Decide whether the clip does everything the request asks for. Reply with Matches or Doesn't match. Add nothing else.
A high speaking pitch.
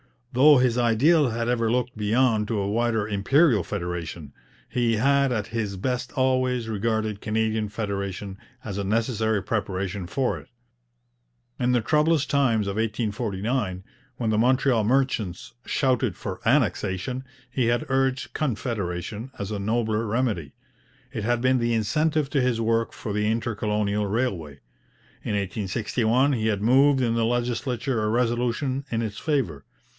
Doesn't match